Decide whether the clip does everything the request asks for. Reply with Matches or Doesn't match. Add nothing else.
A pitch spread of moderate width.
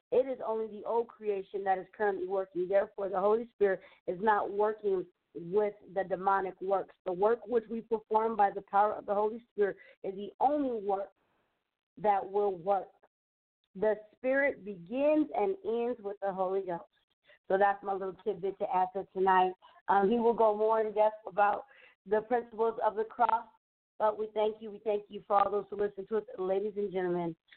Doesn't match